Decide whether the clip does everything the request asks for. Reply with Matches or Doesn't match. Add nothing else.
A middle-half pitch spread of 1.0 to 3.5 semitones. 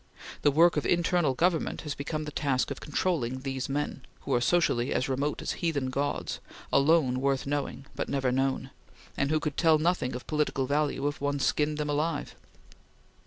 Matches